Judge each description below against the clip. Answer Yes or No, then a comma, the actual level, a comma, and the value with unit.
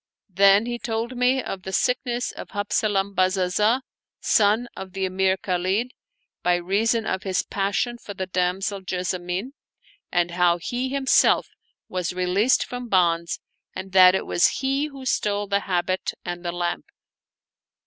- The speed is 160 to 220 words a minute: No, average, 150 wpm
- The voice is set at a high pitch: Yes, high, 195 Hz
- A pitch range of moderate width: Yes, average, 4.2 semitones